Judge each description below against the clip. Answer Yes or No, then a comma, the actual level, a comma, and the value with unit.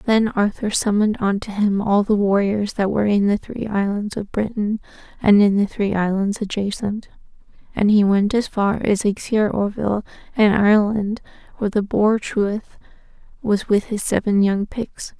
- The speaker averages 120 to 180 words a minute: Yes, average, 165 wpm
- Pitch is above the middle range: Yes, high, 205 Hz